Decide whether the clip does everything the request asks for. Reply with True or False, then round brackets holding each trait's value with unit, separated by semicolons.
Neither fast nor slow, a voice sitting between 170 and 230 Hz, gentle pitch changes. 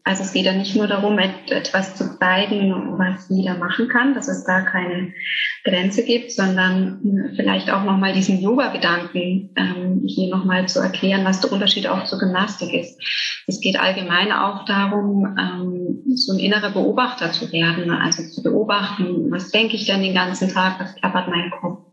True (175 wpm; 190 Hz; 1.9 semitones)